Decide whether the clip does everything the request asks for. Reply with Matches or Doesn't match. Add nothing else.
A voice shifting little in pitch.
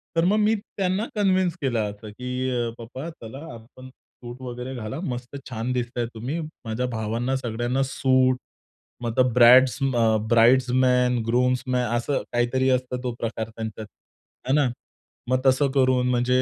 Matches